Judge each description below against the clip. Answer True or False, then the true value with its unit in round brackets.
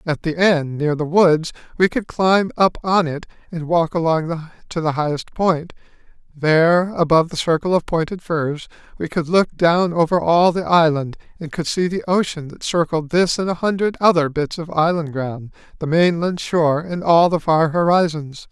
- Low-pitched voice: False (165 Hz)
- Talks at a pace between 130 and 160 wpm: False (190 wpm)